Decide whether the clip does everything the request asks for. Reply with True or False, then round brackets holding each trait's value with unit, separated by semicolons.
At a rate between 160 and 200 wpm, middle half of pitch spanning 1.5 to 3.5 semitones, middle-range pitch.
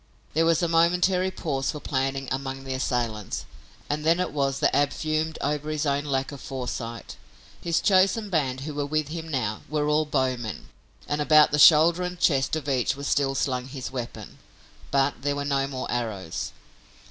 True (185 wpm; 2.9 semitones; 145 Hz)